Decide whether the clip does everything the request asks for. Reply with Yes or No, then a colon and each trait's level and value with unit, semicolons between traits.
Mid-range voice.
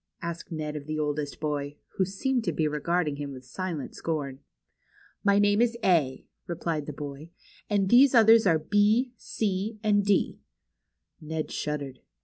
Yes: medium, 165 Hz